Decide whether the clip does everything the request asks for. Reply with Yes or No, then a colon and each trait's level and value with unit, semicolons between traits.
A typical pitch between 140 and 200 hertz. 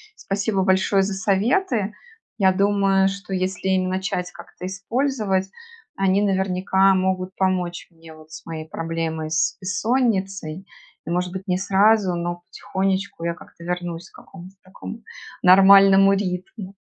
Yes: high, 190 Hz